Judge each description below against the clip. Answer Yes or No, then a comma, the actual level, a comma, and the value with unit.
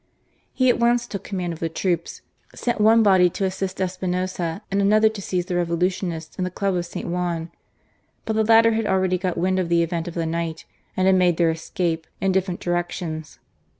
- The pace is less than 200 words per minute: No, fast, 205 wpm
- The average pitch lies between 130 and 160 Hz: No, medium, 180 Hz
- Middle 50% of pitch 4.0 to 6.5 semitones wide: No, narrow, 2.4 semitones